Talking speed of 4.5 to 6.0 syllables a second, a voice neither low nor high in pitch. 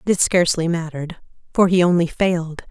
No: 6.3 syllables/s; medium, 170 Hz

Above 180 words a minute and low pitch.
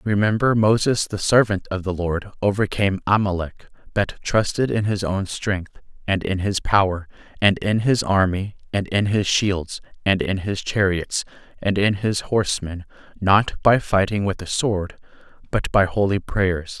No: average, 160 wpm; low, 100 Hz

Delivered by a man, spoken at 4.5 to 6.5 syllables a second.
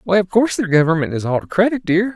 No: male; 6.8 syllables/s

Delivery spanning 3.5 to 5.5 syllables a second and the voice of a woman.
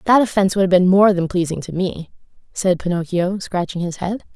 No: 5.7 syllables/s; female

